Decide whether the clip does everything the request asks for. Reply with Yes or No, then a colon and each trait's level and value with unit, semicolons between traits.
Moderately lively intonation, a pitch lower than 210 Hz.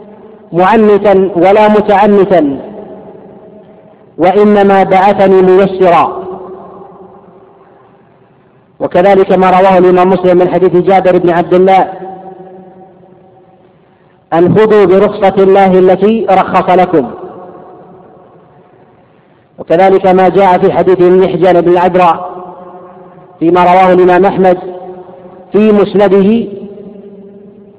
No: narrow, 1.6 semitones; medium, 185 Hz